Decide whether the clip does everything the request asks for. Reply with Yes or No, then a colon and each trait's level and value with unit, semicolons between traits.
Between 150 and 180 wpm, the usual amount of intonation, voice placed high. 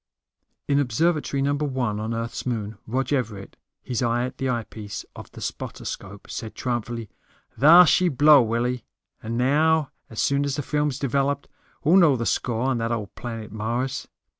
No: average, 175 wpm; average, 3.7 semitones; low, 125 Hz